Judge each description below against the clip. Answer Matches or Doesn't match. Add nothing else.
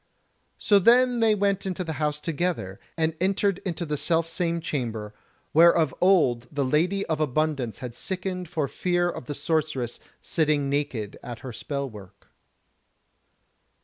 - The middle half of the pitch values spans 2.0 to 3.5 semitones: Doesn't match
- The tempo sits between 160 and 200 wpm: Doesn't match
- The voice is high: Doesn't match